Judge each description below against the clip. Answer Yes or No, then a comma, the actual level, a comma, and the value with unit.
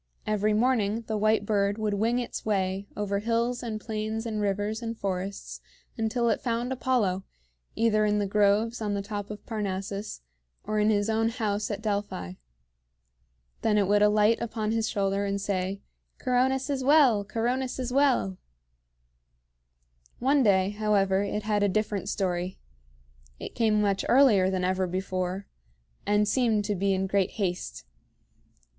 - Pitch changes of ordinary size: No, narrow, 2.3 semitones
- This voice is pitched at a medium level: No, high, 210 Hz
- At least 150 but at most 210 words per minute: Yes, average, 155 wpm